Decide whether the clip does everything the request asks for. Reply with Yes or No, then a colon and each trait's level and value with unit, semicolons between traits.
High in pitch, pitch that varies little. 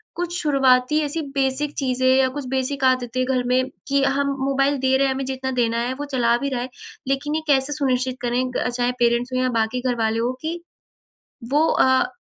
Yes: very high, 260 Hz; narrow, 1.7 semitones